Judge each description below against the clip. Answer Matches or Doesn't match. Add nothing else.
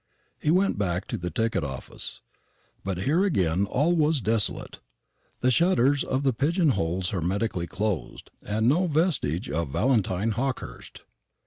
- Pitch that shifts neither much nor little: Doesn't match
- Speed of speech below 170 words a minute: Matches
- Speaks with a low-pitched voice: Matches